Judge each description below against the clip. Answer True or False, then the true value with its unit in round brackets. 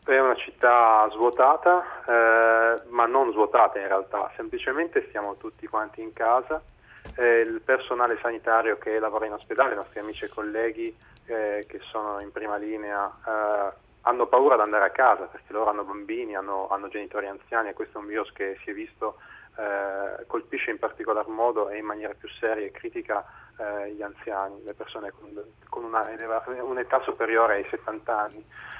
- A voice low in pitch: True (115 Hz)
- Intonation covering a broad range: False (2.8 semitones)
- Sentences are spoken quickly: True (175 wpm)